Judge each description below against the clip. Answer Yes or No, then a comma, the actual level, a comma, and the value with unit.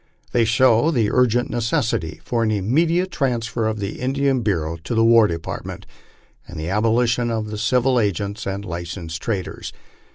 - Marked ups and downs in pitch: No, average, 3.7 semitones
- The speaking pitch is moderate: No, low, 115 Hz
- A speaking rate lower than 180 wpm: Yes, average, 165 wpm